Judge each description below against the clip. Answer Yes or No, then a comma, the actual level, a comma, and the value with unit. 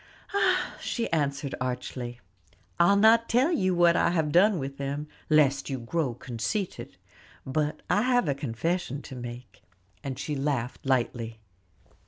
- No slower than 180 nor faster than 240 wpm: No, average, 145 wpm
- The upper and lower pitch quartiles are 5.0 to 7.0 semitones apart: Yes, wide, 5.6 semitones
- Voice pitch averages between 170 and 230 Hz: No, medium, 145 Hz